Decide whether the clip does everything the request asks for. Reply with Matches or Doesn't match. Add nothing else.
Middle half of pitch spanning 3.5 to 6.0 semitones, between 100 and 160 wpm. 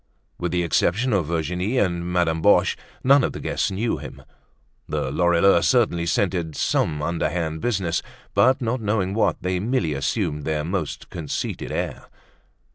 Matches